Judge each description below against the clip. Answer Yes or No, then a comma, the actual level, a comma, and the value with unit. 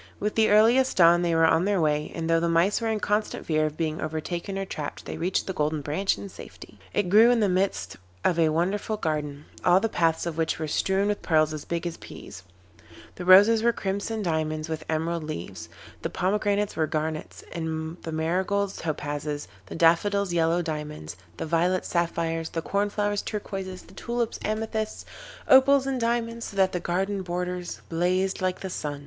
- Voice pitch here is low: No, medium, 175 Hz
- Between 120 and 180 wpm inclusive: No, average, 190 wpm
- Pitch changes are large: No, average, 4.1 semitones